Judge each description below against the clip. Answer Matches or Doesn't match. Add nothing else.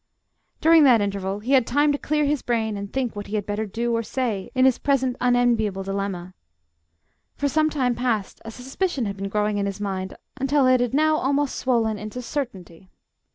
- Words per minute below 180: Doesn't match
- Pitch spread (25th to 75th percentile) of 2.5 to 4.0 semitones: Doesn't match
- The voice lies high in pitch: Matches